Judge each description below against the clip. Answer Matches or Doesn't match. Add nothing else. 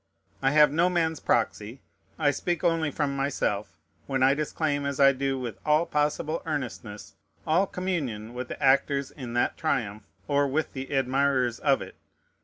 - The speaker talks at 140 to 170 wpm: Matches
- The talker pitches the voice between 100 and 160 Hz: Matches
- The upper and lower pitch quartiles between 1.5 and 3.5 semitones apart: Matches